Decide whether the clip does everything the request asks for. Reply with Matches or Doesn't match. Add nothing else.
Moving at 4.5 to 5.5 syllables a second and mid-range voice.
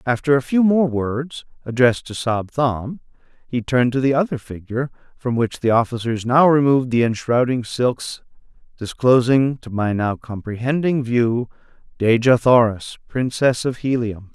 Doesn't match